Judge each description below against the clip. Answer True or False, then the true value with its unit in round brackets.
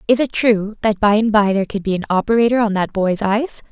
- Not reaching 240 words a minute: False (260 wpm)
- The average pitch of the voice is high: True (210 Hz)